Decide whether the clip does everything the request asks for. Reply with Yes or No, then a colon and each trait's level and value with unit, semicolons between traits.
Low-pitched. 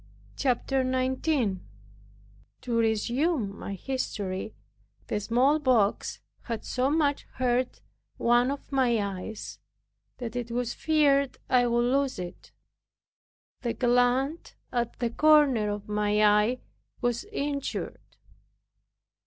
No: high, 245 Hz